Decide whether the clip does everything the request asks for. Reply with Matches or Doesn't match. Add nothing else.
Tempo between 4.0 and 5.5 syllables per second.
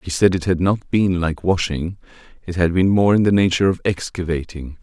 Matches